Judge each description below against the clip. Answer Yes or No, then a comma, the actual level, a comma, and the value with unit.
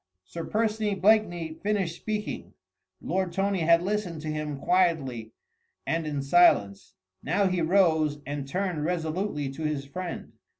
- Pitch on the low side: No, medium, 170 Hz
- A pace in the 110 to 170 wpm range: Yes, slow, 135 wpm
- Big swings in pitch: No, average, 4.2 semitones